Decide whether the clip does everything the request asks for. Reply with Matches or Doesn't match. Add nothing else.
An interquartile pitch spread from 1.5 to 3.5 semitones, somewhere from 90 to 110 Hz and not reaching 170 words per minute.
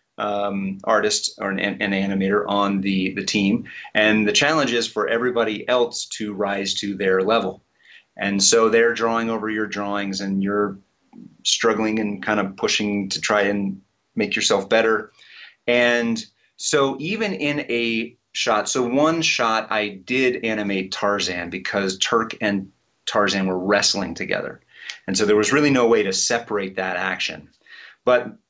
Matches